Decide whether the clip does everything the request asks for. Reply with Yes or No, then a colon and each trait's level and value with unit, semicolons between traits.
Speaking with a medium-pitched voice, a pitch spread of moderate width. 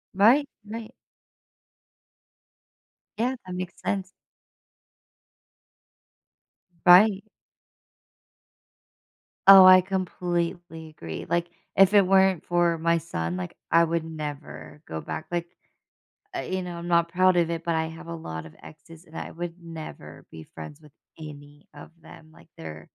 Yes: medium, 170 Hz; average, 3.3 semitones